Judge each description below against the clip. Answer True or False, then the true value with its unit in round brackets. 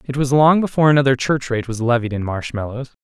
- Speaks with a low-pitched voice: True (130 Hz)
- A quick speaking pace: True (220 wpm)